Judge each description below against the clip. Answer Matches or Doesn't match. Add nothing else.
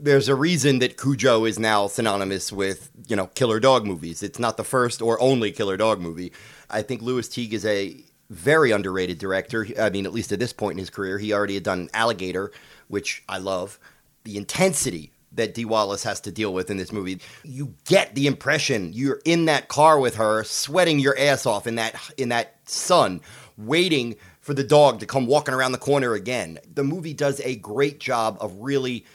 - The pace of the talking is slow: Doesn't match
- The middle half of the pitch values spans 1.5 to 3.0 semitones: Doesn't match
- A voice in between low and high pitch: Doesn't match